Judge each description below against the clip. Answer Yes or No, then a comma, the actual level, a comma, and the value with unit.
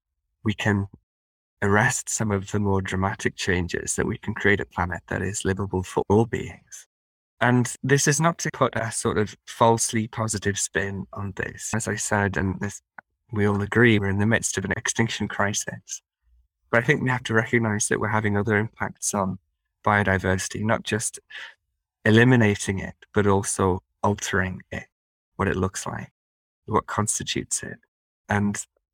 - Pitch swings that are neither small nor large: Yes, average, 3.0 semitones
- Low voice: Yes, low, 100 Hz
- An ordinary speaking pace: Yes, average, 170 wpm